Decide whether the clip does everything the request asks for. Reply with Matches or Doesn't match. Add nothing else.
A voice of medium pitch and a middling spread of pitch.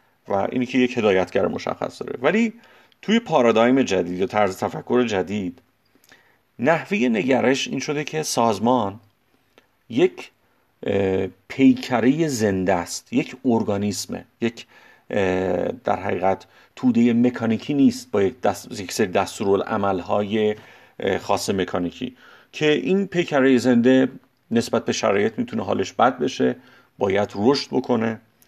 Doesn't match